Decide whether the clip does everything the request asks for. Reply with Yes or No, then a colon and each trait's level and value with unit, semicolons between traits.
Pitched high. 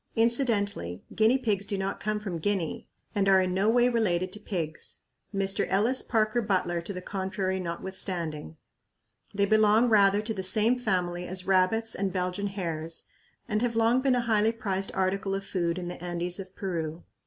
Yes: high, 195 Hz